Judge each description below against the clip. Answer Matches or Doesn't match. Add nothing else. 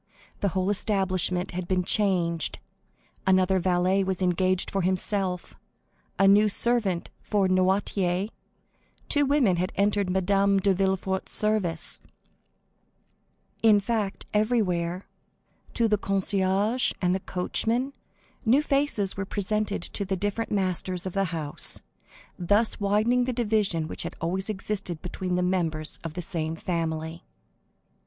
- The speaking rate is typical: Doesn't match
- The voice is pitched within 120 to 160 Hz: Doesn't match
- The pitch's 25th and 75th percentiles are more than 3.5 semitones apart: Doesn't match